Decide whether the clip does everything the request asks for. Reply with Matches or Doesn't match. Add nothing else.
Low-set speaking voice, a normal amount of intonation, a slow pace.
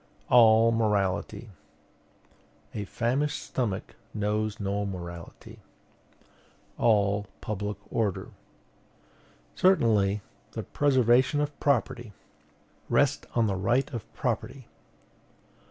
Matches